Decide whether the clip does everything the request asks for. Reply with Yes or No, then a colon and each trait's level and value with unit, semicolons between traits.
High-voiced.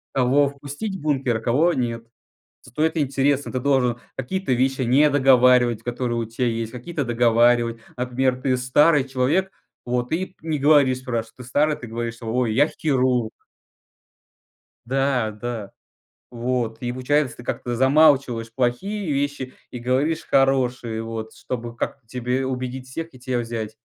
No: low, 125 Hz